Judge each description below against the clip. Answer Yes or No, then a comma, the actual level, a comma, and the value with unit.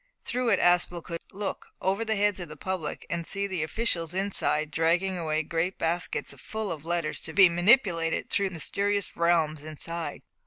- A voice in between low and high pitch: Yes, medium, 175 Hz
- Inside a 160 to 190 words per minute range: Yes, average, 180 wpm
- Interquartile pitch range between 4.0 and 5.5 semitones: No, average, 3.3 semitones